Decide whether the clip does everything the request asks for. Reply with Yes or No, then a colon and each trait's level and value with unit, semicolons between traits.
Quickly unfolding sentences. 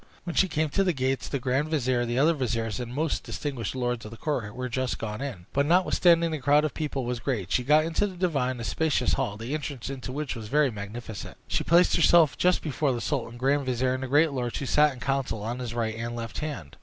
Yes: fast, 245 wpm